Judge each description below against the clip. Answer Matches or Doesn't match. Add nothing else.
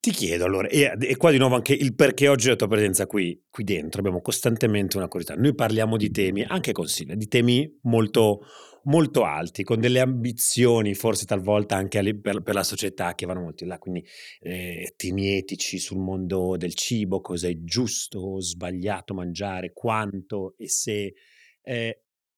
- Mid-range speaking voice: Doesn't match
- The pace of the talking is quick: Matches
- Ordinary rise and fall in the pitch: Matches